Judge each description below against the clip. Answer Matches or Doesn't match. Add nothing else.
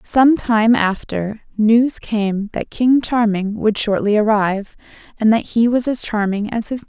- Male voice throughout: Doesn't match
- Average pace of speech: Matches